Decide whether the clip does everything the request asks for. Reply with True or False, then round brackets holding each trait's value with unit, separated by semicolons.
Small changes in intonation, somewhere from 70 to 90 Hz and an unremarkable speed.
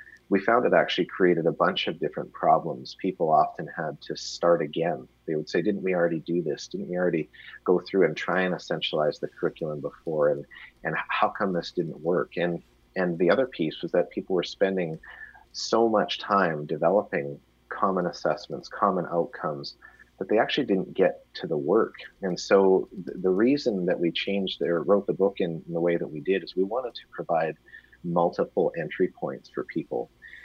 True (2.1 semitones; 85 Hz; 195 wpm)